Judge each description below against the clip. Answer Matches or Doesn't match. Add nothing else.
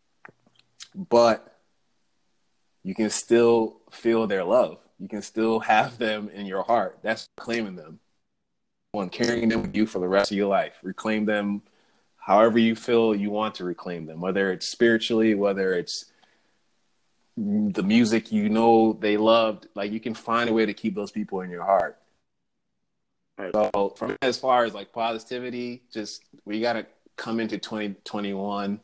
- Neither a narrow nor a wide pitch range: Doesn't match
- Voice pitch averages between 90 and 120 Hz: Matches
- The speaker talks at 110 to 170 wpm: Matches